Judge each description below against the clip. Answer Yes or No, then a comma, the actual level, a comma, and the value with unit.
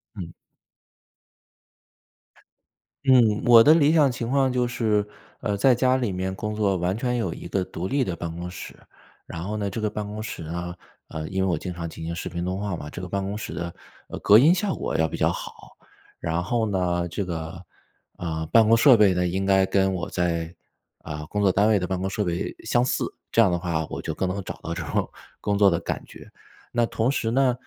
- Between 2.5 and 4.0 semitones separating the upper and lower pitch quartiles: No, average, 4.5 semitones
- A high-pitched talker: No, very low, 95 Hz